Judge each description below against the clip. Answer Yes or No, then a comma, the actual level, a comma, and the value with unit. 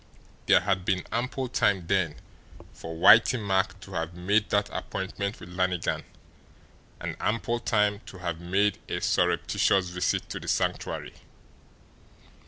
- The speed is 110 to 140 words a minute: Yes, slow, 135 wpm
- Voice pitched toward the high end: No, very low, 95 Hz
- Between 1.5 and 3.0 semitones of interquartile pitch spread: Yes, narrow, 2.6 semitones